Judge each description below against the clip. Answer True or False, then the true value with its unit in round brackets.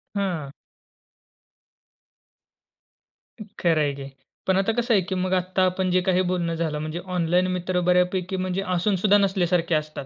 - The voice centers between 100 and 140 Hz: False (180 Hz)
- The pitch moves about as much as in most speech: False (2.1 semitones)